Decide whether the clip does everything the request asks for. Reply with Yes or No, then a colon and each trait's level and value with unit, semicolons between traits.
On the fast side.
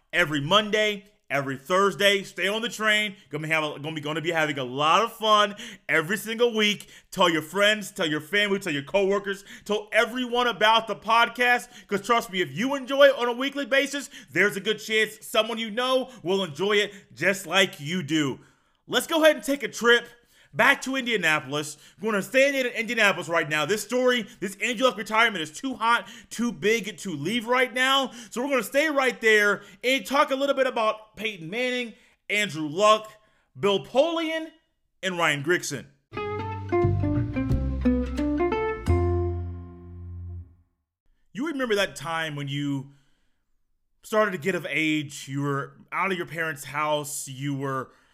No: average, 170 wpm